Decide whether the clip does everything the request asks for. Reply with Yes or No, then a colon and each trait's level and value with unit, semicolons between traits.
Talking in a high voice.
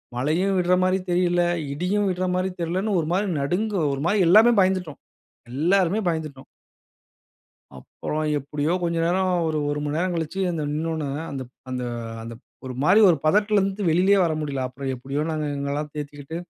No: medium, 165 Hz